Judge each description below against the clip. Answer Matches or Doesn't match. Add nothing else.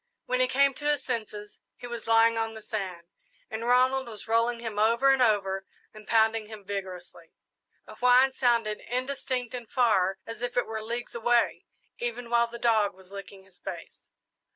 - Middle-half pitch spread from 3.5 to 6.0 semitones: Doesn't match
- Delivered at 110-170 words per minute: Doesn't match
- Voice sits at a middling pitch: Doesn't match